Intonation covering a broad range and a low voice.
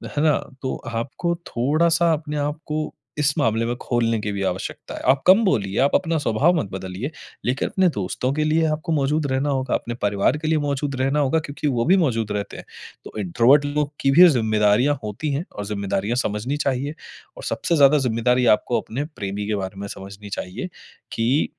Yes: wide, 5.7 semitones; low, 130 Hz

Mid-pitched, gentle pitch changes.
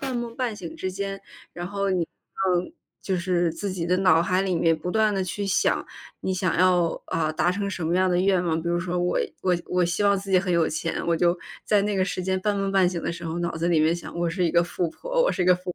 Yes: medium, 180 Hz; narrow, 2.2 semitones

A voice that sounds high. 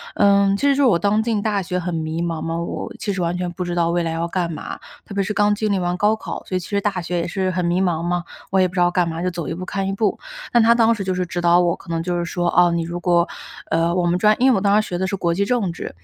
No: medium, 180 Hz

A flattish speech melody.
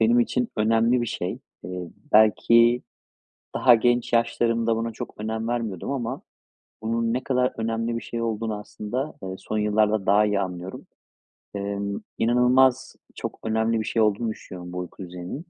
Yes: narrow, 2.3 semitones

